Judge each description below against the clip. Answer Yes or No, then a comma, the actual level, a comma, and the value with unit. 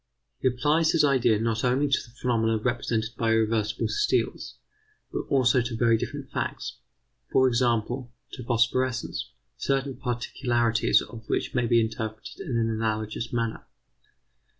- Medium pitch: No, low, 120 Hz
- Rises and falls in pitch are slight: Yes, narrow, 2.3 semitones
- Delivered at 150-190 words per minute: No, average, 140 wpm